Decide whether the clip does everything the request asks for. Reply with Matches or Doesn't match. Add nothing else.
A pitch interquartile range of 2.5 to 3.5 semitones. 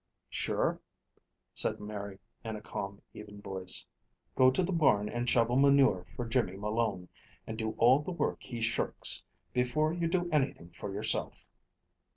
Doesn't match